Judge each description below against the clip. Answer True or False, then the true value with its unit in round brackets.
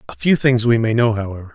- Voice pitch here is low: True (115 Hz)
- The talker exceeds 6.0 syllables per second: True (6.5 syllables/s)